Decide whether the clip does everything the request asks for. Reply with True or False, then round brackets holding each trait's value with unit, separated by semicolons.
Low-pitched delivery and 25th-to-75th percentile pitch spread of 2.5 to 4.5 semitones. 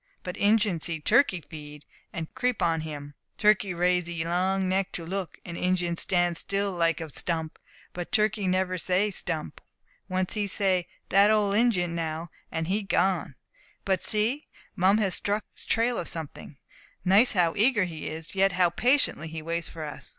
False (180 Hz; 3.3 semitones)